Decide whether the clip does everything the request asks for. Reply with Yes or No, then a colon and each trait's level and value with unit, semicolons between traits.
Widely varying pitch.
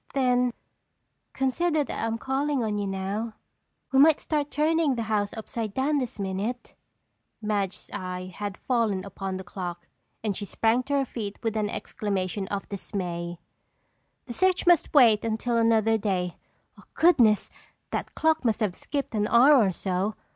No: average, 4.9 semitones